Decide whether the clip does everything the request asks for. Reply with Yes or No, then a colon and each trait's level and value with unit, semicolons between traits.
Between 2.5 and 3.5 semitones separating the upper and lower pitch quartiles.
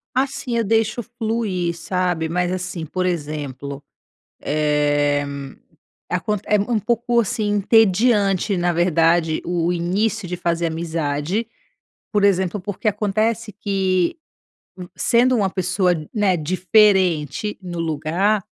No: average, 4.1 semitones